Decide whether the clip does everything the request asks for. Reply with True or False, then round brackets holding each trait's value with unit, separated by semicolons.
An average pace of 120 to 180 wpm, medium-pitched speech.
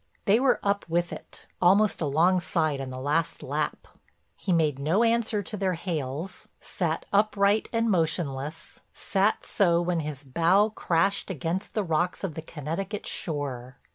True (150 wpm; 175 Hz)